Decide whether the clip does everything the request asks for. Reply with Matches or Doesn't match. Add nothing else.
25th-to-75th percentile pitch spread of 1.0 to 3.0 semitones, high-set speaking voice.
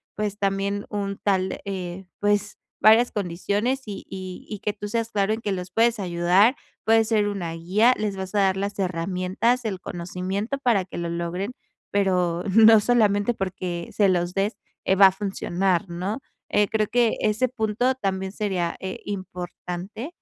Matches